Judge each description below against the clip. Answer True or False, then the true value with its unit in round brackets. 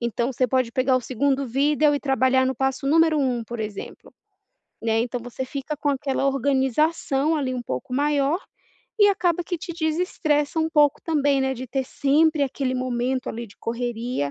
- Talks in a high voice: True (270 Hz)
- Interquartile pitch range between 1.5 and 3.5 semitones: True (3.0 semitones)